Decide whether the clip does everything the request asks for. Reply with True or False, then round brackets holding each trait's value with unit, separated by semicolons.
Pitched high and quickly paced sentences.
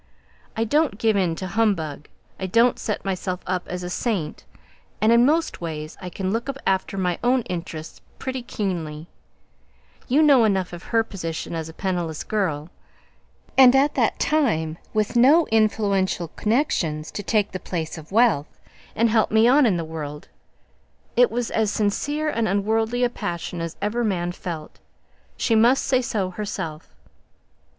False (200 Hz; 160 wpm)